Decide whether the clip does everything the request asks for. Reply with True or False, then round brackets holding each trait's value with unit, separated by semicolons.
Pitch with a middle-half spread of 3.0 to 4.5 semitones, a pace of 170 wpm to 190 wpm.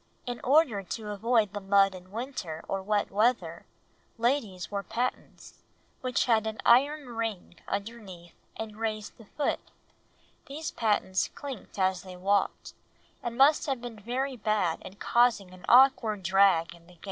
False (4.1 semitones; 155 wpm)